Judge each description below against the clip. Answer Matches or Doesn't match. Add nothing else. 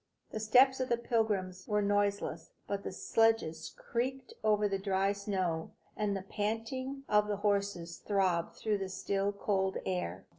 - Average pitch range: Doesn't match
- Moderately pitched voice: Doesn't match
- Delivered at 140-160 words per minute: Matches